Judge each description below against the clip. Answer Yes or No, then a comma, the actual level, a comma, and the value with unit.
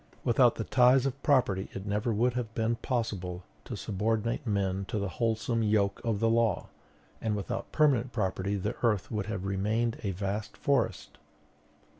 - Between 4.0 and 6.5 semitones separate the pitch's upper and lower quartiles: No, average, 3.0 semitones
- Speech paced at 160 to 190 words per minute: Yes, average, 165 wpm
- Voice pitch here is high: No, low, 110 Hz